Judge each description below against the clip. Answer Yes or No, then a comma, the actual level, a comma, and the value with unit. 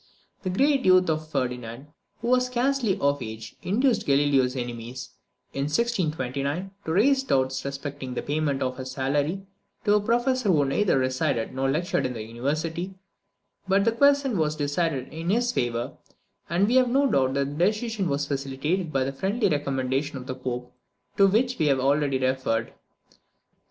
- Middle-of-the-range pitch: Yes, medium, 145 Hz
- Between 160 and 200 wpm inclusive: Yes, average, 165 wpm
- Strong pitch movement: Yes, wide, 7.1 semitones